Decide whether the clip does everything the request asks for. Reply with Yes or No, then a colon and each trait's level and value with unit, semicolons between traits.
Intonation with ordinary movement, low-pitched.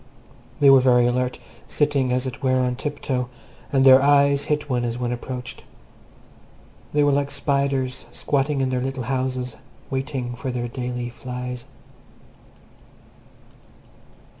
No: narrow, 1.8 semitones; low, 130 Hz